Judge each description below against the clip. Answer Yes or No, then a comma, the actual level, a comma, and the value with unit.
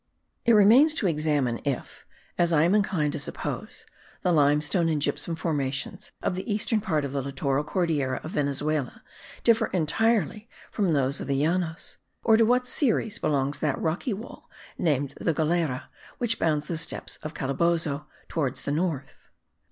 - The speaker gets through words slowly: No, average, 160 wpm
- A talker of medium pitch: Yes, medium, 160 Hz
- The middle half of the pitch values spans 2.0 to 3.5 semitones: No, average, 5.2 semitones